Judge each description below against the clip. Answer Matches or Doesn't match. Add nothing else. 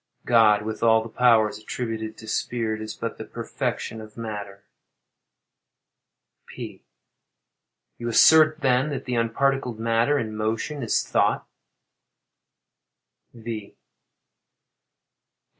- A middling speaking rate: Doesn't match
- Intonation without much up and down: Matches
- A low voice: Matches